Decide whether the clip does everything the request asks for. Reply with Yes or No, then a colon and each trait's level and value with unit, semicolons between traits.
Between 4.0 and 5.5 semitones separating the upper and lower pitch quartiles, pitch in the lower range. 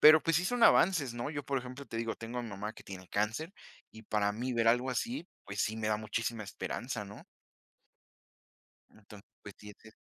Yes: average, 4.3 semitones; low, 115 Hz